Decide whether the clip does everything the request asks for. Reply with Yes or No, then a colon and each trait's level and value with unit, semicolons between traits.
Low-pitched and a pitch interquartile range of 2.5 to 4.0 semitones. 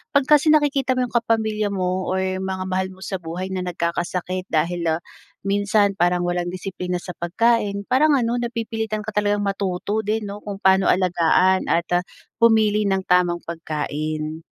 No: high, 190 Hz; average, 3.5 semitones